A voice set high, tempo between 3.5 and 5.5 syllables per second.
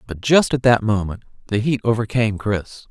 No: low, 110 Hz; 5.3 syllables/s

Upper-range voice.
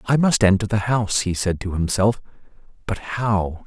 No: low, 105 Hz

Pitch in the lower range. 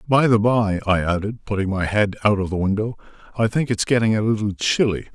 Yes: low, 105 Hz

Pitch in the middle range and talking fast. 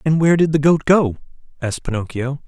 No: medium, 145 Hz; average, 195 wpm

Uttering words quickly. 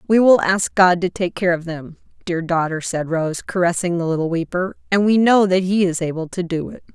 Yes: fast, 235 wpm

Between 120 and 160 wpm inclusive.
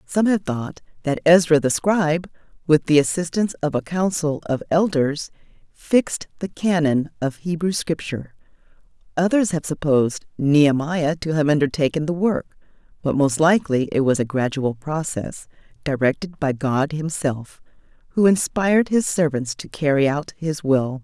Yes: average, 145 wpm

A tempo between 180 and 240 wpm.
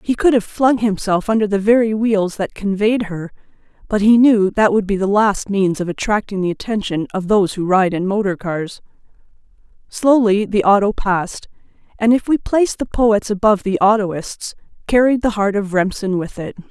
Yes: average, 185 wpm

